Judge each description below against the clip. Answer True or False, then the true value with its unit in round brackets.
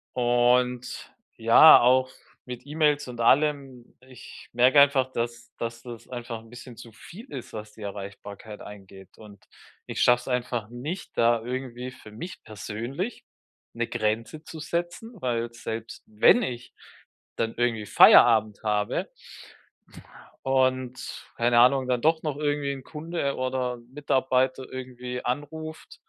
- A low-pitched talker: True (125 Hz)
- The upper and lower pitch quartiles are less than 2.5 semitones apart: False (2.8 semitones)